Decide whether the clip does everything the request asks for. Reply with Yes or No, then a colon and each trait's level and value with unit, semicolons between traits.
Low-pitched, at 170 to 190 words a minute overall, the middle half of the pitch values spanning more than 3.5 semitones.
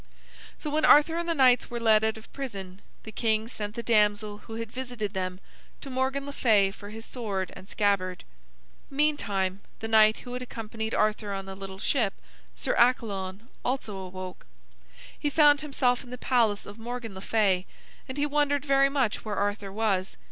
No: high, 220 Hz; average, 185 wpm; average, 4.3 semitones